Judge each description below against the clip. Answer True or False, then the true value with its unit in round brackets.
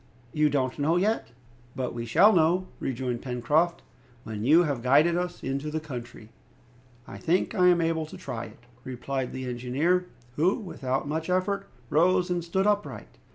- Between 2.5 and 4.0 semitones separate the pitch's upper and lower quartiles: False (5.6 semitones)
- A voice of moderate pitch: True (155 Hz)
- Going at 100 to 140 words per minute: False (165 wpm)